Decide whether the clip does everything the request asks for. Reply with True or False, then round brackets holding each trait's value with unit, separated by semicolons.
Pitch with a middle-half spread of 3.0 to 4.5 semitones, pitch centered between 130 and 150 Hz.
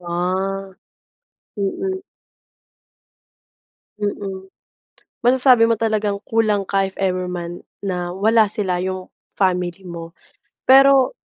False (3.5 semitones; 195 Hz)